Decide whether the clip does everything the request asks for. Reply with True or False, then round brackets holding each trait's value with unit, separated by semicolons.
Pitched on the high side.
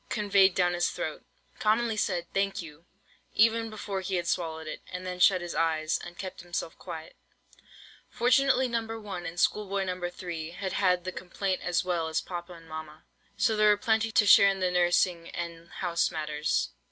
False (180 Hz)